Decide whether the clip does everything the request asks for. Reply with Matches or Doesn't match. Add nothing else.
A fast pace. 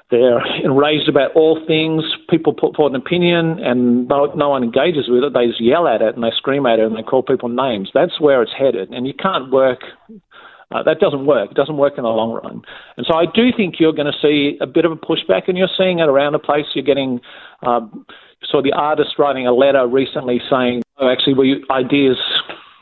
Matches